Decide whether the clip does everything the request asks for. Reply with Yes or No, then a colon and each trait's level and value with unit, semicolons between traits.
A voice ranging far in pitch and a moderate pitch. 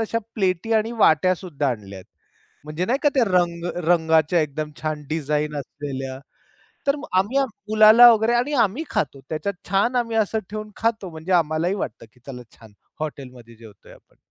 Yes: wide, 6.6 semitones; medium, 170 Hz